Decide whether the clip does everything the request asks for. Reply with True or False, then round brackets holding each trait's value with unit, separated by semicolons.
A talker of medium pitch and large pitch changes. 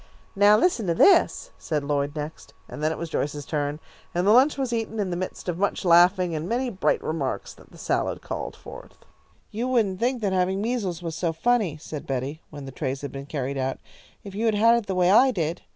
True (180 Hz; 6.3 semitones)